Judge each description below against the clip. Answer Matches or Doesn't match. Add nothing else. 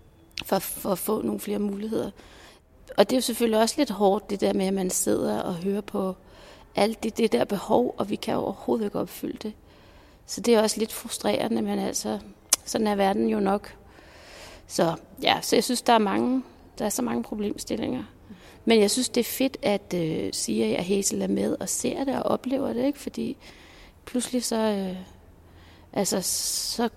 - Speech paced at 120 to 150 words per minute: Doesn't match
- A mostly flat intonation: Doesn't match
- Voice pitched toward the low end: Doesn't match